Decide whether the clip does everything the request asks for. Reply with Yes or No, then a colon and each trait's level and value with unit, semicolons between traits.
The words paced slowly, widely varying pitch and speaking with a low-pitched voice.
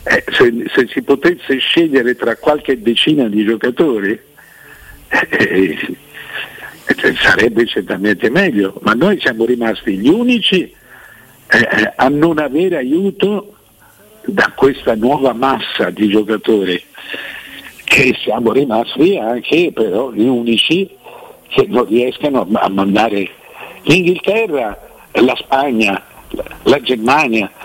Yes: slow, 110 wpm; wide, 7.4 semitones; low, 130 Hz